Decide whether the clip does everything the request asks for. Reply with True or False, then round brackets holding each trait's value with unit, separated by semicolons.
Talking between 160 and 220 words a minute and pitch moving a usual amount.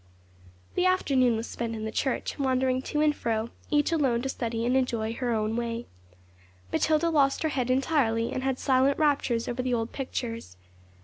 True (185 wpm; 3.1 semitones)